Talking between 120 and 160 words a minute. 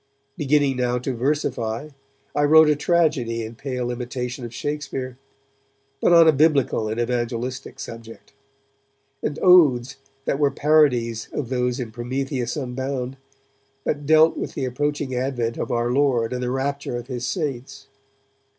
Yes: average, 145 wpm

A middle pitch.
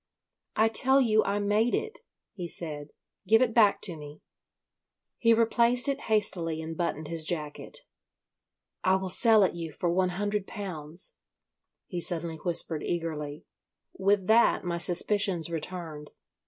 Yes: medium, 180 Hz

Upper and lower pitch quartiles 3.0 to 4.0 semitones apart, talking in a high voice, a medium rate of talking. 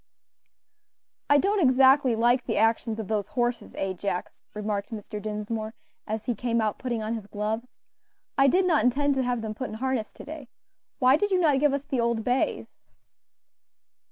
Yes: average, 3.7 semitones; high, 240 Hz; average, 180 wpm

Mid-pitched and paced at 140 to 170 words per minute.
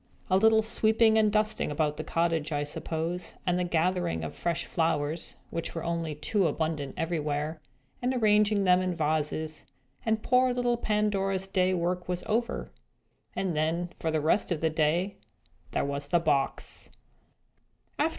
Yes: medium, 175 Hz; average, 155 wpm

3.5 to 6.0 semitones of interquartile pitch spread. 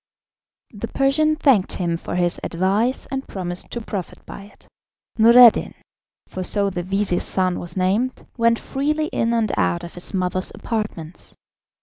Yes: average, 4.7 semitones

